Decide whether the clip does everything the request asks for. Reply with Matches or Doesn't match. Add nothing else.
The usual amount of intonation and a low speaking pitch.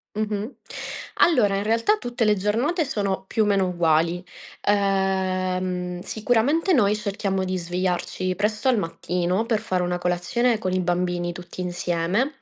Doesn't match